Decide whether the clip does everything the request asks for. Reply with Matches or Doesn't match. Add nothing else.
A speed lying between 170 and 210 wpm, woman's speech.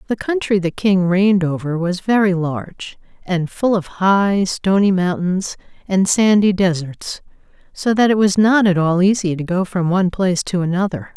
Matches